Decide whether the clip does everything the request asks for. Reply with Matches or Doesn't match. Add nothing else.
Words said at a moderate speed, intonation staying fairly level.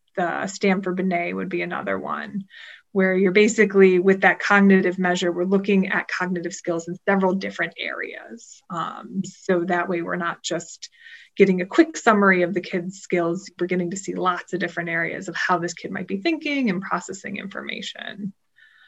Matches